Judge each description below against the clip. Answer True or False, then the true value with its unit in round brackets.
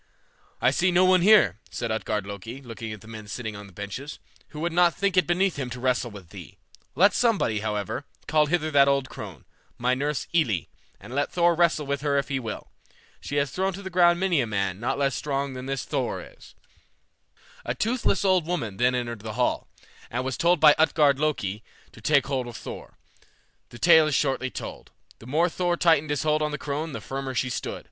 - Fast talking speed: True (215 wpm)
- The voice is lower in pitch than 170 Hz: True (140 Hz)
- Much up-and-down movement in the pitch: True (5.9 semitones)